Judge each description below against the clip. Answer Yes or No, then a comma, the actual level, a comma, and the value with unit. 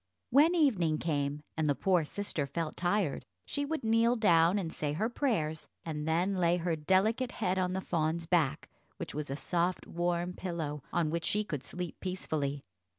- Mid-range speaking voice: Yes, medium, 175 Hz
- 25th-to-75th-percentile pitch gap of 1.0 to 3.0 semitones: No, average, 4.1 semitones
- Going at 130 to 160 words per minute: No, average, 180 wpm